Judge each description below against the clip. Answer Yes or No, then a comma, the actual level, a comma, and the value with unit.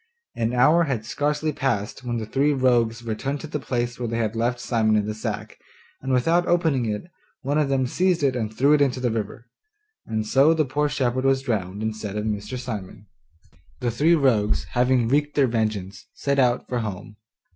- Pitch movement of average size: Yes, average, 4.0 semitones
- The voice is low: Yes, low, 125 Hz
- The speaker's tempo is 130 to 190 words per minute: No, average, 200 wpm